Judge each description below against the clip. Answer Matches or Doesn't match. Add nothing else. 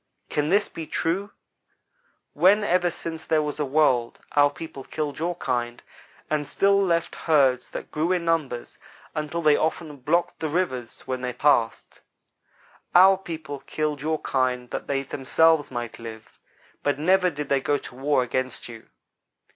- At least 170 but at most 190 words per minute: Doesn't match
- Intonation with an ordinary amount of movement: Matches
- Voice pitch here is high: Doesn't match